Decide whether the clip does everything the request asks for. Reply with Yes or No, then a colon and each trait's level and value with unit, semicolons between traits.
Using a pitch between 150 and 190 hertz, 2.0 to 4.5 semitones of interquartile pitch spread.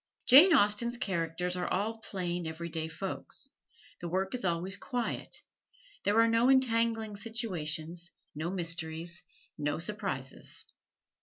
No: medium, 185 Hz; average, 5.2 semitones